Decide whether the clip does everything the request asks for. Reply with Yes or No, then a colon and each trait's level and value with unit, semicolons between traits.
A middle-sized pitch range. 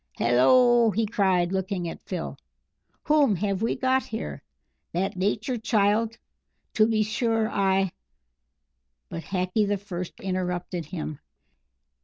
Yes: average, 4.0 semitones